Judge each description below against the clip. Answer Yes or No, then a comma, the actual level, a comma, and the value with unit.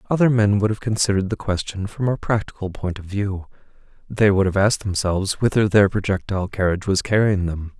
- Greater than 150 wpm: Yes, average, 190 wpm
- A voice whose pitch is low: Yes, low, 100 Hz